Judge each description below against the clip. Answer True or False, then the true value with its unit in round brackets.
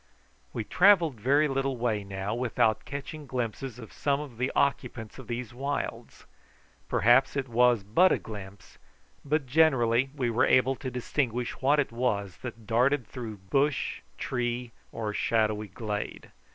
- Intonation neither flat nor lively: True (3.4 semitones)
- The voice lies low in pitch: True (125 Hz)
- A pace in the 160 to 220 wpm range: False (150 wpm)